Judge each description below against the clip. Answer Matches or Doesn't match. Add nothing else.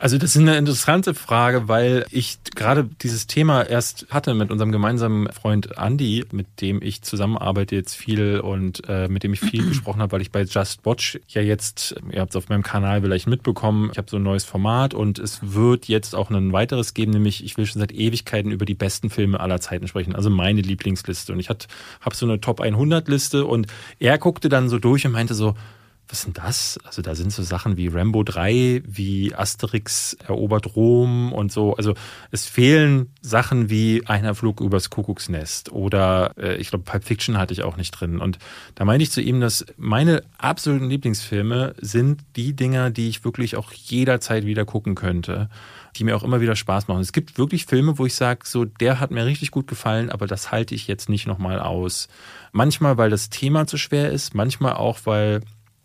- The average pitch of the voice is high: Doesn't match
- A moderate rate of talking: Doesn't match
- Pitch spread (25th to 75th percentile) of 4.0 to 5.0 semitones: Doesn't match